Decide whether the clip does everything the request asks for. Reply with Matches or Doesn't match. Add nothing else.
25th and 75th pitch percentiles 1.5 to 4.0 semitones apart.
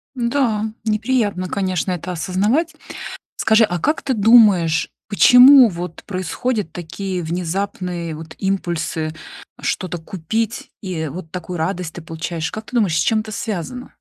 Doesn't match